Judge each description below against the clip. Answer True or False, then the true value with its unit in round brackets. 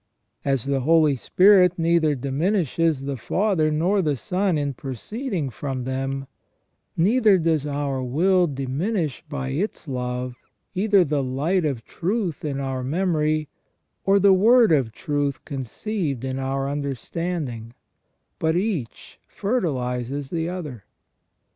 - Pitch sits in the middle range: True (150 Hz)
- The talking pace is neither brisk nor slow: False (125 wpm)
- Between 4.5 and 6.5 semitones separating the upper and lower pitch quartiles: True (5.2 semitones)